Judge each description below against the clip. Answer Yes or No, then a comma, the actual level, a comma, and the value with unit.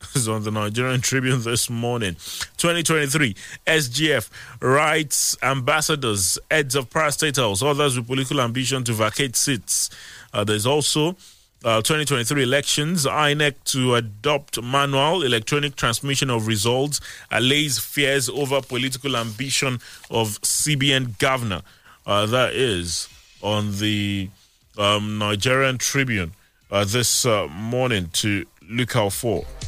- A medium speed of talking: No, slow, 125 wpm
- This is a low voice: Yes, low, 130 Hz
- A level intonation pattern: No, average, 4.6 semitones